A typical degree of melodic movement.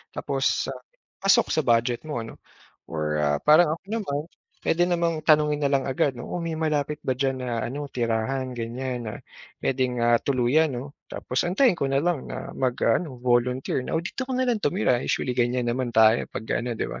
Yes: average, 4.2 semitones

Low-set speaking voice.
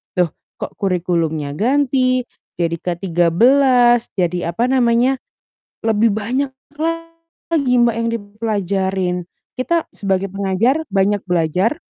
No: high, 215 Hz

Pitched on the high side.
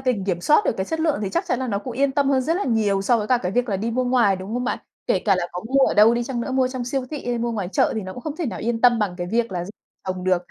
Yes: high, 235 Hz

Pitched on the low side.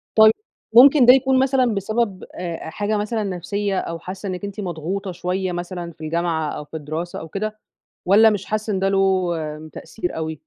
No: high, 195 Hz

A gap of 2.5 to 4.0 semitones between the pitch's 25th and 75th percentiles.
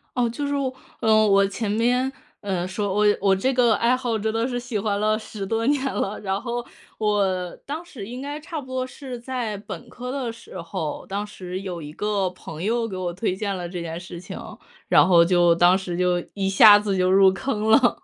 No: average, 4.4 semitones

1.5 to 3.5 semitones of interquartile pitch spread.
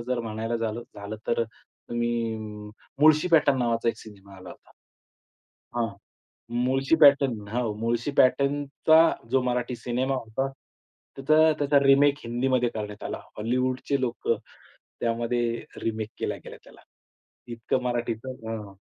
Yes: average, 2.9 semitones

